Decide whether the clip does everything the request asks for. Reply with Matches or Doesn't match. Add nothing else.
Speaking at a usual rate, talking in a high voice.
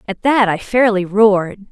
Matches